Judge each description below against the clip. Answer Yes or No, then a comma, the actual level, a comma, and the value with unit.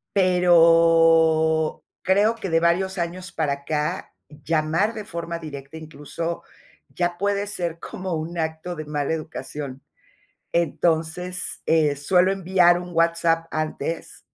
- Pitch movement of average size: No, narrow, 2.1 semitones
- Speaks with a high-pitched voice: No, medium, 165 Hz